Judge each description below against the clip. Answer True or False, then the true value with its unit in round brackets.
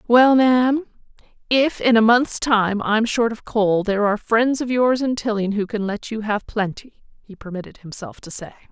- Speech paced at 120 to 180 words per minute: False (200 wpm)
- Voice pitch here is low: False (220 Hz)